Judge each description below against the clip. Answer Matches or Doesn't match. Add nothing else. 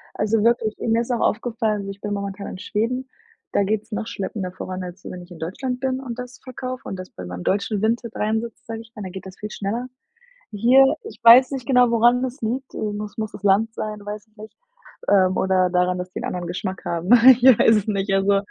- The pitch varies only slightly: Doesn't match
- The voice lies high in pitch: Matches